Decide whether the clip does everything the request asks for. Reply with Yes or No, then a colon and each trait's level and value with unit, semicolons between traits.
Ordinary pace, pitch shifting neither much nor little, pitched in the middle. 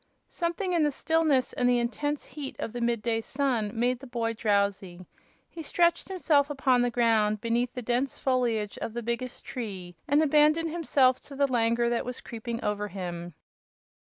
No: average, 180 wpm; average, 3.9 semitones; high, 245 Hz